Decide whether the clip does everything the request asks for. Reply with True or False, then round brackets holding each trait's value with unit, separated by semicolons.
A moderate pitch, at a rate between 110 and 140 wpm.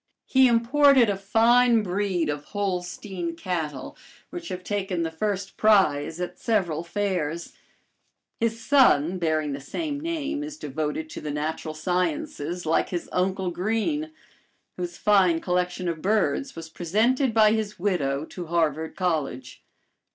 True (180 Hz; 135 wpm)